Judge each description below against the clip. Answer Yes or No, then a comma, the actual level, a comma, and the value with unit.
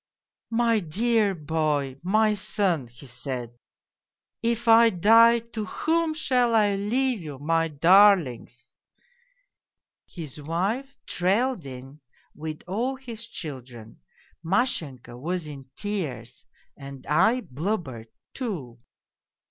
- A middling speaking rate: No, slow, 120 wpm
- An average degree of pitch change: No, wide, 8.2 semitones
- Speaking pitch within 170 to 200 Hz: Yes, medium, 185 Hz